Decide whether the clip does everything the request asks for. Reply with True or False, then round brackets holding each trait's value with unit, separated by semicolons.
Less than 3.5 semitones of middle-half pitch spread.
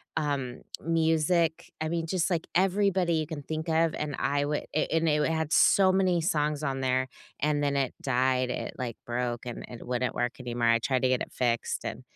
False (4.2 semitones)